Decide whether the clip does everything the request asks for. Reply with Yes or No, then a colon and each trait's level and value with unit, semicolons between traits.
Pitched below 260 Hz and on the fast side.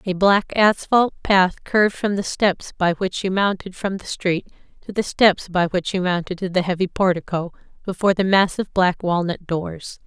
No: medium, 185 Hz; average, 190 wpm